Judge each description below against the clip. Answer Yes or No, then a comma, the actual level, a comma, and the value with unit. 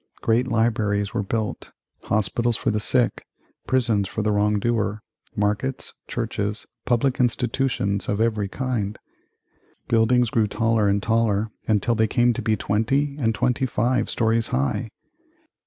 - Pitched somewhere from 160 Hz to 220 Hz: No, low, 110 Hz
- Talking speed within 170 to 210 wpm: No, average, 140 wpm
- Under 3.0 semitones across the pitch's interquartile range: Yes, narrow, 2.5 semitones